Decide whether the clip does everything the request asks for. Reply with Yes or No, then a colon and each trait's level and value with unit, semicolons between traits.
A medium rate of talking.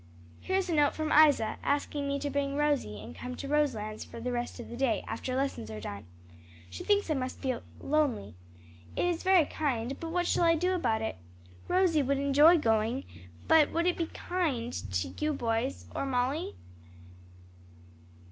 Yes: average, 185 wpm